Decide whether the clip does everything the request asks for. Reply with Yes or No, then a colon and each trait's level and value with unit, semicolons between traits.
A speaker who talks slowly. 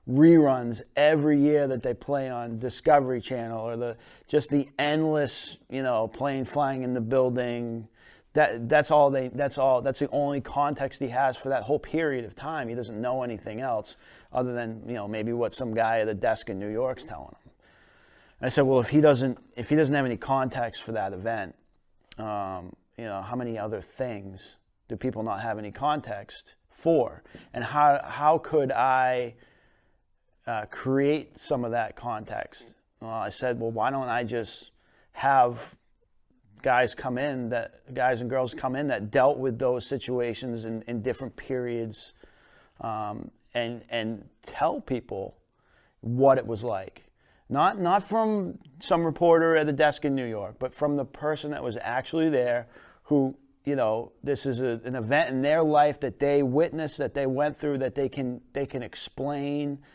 No: average, 180 wpm